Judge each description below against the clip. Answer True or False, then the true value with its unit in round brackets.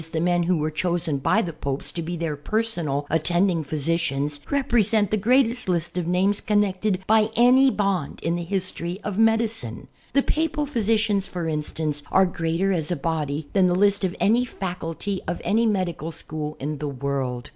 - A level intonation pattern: False (5.0 semitones)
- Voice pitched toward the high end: False (180 Hz)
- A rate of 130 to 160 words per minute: False (180 wpm)